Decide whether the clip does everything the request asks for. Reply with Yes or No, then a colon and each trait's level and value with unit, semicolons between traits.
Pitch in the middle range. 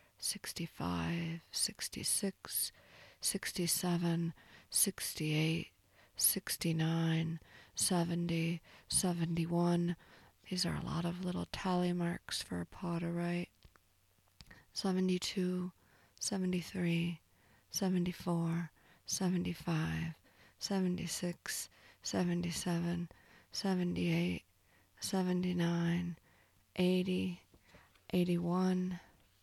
Yes: medium, 170 Hz